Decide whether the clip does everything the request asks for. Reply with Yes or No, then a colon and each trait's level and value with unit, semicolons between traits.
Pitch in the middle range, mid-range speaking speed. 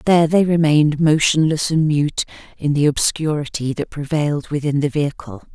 Yes: medium, 150 Hz; average, 150 wpm